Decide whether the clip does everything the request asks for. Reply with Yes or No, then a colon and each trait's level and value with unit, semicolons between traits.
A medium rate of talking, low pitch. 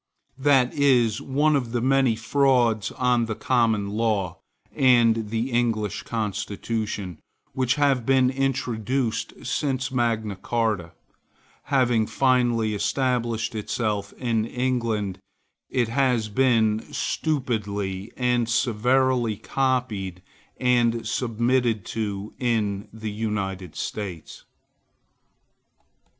No: slow, 95 wpm; low, 115 Hz